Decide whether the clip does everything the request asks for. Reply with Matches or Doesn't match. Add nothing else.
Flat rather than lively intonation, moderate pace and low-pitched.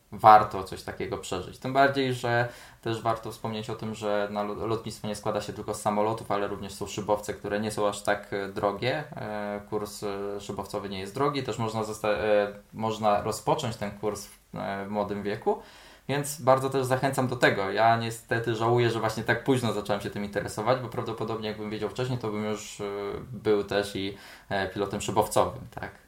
Doesn't match